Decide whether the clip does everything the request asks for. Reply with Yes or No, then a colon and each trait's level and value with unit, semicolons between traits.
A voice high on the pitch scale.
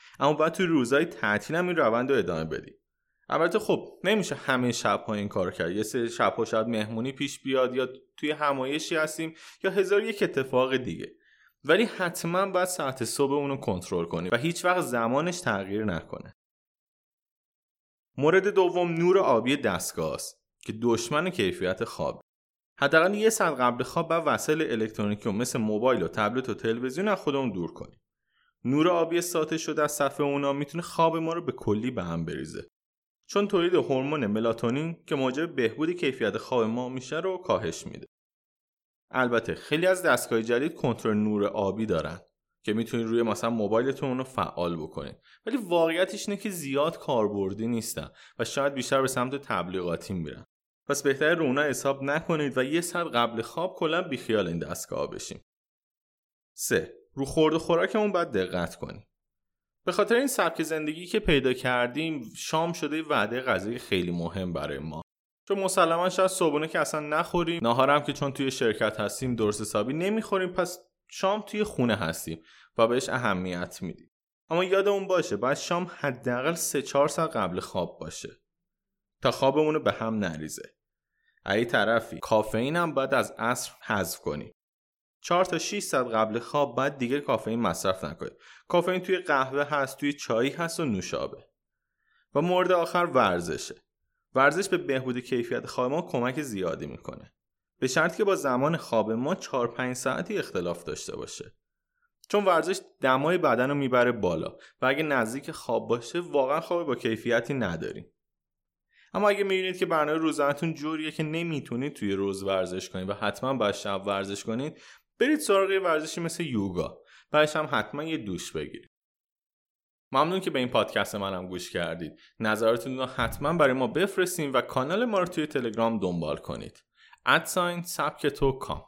No: medium, 140 Hz